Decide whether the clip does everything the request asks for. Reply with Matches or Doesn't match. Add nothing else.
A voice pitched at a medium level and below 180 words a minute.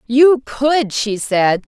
Doesn't match